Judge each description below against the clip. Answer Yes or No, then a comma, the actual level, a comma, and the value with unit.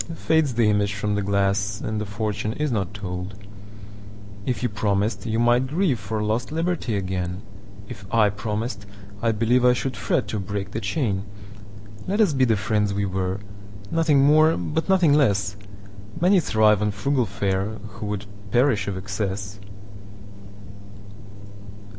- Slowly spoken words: Yes, slow, 130 wpm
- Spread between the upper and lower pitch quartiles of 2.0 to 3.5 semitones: Yes, average, 2.9 semitones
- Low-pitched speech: Yes, low, 105 Hz